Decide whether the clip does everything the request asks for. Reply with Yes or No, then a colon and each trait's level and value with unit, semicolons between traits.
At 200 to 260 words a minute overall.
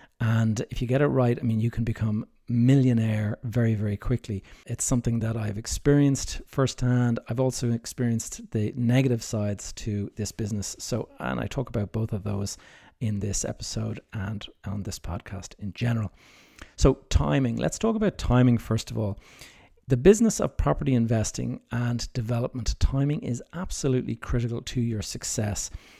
No: average, 165 wpm